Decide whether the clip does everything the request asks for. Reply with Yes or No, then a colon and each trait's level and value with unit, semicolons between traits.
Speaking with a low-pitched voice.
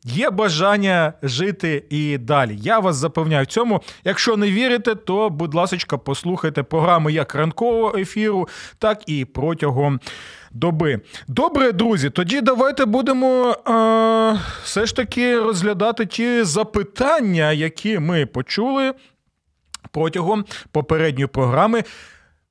No: high, 190 Hz